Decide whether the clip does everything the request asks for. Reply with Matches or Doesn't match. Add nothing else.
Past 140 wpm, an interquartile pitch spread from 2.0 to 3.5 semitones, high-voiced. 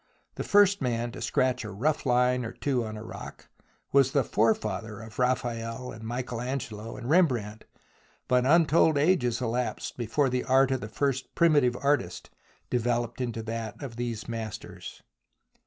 Doesn't match